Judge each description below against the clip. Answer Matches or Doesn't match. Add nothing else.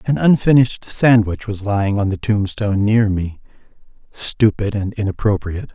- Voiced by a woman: Doesn't match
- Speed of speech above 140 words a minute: Doesn't match